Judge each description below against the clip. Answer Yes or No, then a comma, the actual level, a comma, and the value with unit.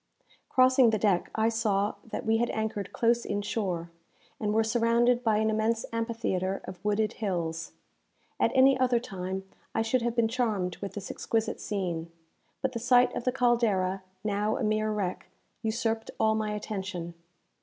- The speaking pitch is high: Yes, high, 220 Hz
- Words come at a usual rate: Yes, average, 165 wpm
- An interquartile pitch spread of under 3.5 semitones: Yes, average, 2.8 semitones